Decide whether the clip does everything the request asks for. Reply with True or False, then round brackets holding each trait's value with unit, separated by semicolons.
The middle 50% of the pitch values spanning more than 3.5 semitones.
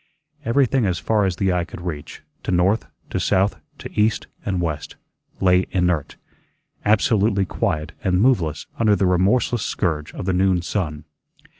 False (3.1 semitones)